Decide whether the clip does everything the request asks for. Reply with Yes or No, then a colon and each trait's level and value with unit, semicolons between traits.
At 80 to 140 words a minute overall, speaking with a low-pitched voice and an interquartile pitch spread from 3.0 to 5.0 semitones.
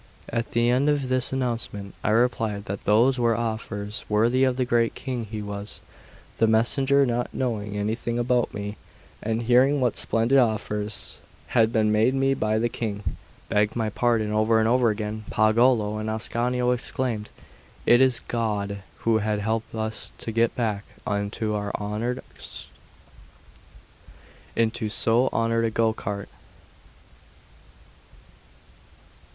No: slow, 135 wpm; low, 115 Hz; narrow, 2.4 semitones